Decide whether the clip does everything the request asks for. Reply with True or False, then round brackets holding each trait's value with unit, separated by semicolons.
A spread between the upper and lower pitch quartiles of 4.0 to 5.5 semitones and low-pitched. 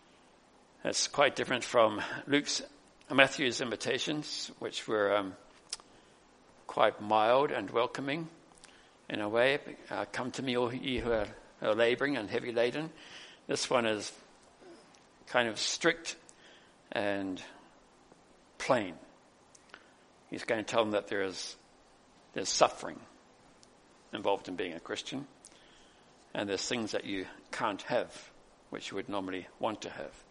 True (5.0 semitones; 120 Hz)